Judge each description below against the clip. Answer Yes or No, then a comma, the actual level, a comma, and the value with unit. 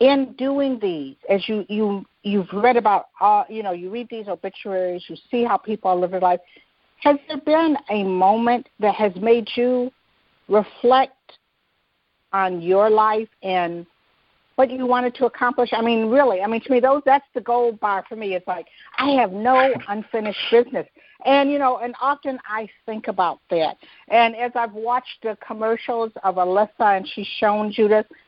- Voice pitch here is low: No, high, 225 Hz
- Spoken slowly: No, average, 180 wpm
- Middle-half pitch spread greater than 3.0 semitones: Yes, average, 3.7 semitones